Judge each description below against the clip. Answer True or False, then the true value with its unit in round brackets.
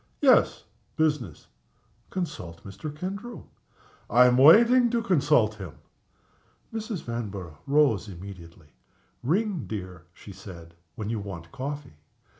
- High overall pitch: False (120 Hz)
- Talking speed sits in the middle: False (110 wpm)